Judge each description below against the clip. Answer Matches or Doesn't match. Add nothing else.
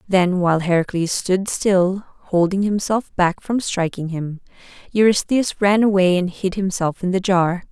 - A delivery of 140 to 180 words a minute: Matches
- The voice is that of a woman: Matches